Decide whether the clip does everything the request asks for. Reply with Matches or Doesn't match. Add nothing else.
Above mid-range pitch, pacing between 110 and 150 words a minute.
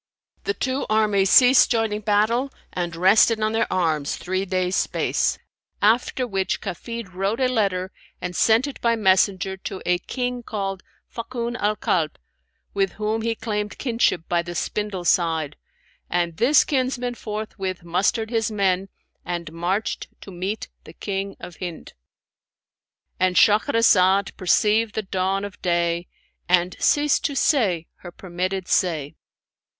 Matches